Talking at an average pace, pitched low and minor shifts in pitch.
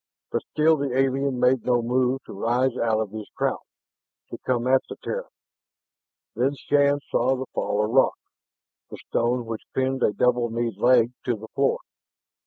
Yes: average, 175 wpm; low, 125 Hz; narrow, 2.2 semitones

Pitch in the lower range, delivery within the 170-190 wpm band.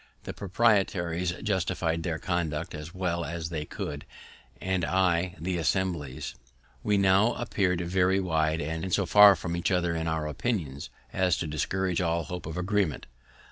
No: very low, 85 Hz; average, 155 wpm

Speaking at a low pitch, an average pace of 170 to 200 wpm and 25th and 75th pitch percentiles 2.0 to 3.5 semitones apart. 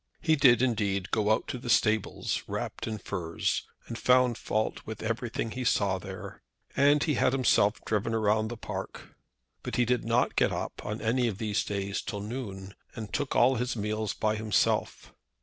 Yes: low, 110 Hz; average, 185 wpm; average, 2.9 semitones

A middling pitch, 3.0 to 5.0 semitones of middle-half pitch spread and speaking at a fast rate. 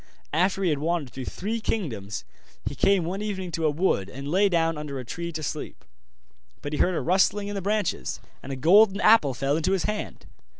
No: medium, 170 Hz; wide, 5.5 semitones; fast, 215 wpm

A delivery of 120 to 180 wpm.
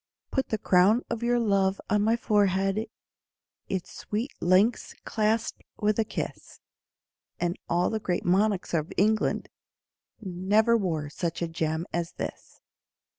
Yes: slow, 135 wpm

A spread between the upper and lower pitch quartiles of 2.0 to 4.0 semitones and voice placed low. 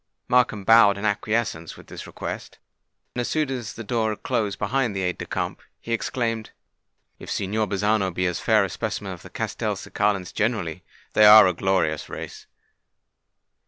Yes: average, 3.0 semitones; low, 105 Hz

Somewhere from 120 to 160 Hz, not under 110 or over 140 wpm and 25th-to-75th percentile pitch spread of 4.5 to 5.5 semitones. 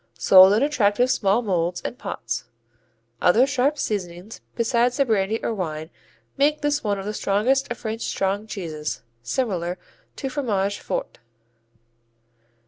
No: high, 210 Hz; slow, 135 wpm; average, 5.0 semitones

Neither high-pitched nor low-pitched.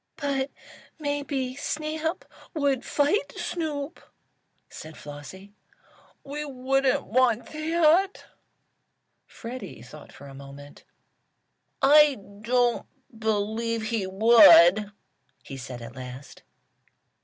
No: high, 245 Hz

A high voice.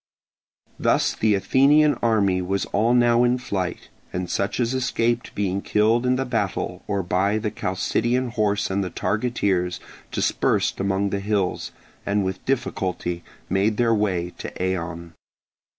No: low, 100 Hz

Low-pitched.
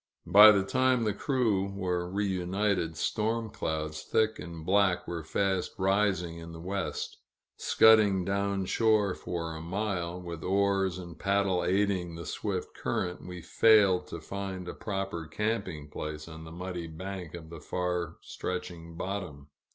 Yes: very low, 95 Hz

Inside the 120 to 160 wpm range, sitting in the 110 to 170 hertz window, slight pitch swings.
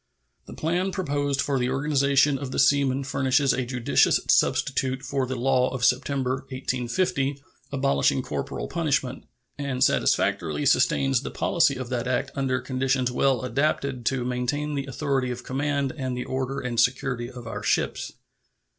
Yes: average, 155 wpm; low, 135 Hz; narrow, 1.8 semitones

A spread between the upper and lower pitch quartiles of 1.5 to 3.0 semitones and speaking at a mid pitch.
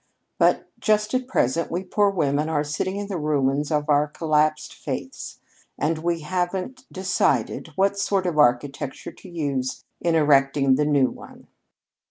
No: average, 4.5 semitones; medium, 155 Hz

